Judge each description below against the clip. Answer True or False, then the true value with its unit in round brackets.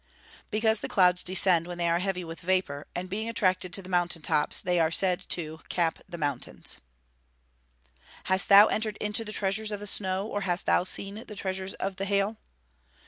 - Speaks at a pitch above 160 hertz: True (185 Hz)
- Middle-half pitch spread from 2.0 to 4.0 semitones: True (2.5 semitones)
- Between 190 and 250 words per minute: True (200 wpm)